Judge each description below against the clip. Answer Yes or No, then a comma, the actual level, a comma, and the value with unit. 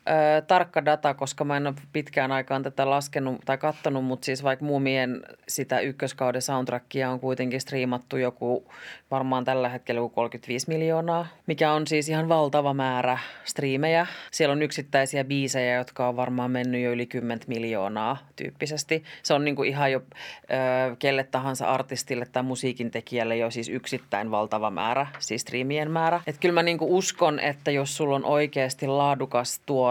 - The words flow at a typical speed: No, fast, 170 wpm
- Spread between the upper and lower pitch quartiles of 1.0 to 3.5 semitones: Yes, average, 2.8 semitones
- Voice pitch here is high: No, low, 135 Hz